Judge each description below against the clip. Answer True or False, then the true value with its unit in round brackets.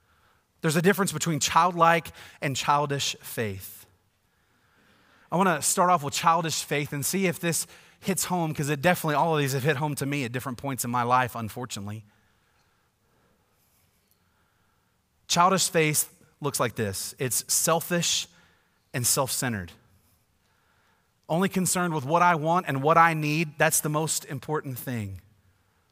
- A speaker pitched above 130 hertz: True (140 Hz)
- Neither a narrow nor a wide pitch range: False (6.6 semitones)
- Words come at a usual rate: True (150 wpm)